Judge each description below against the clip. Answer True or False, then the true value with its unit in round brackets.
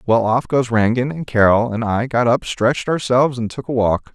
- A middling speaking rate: False (230 wpm)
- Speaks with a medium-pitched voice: False (120 Hz)